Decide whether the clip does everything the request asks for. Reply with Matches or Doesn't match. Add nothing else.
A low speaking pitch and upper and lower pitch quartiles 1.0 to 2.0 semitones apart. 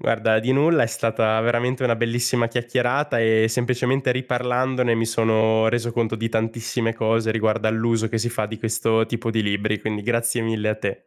Matches